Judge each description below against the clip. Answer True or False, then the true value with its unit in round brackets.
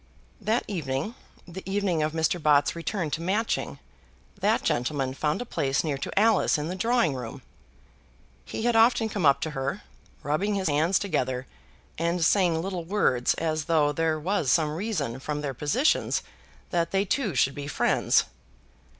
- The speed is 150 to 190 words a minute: True (165 wpm)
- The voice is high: False (165 Hz)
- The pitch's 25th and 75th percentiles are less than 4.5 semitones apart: False (5.3 semitones)